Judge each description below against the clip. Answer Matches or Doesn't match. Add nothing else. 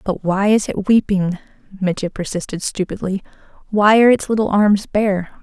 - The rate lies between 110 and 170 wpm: Matches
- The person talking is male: Doesn't match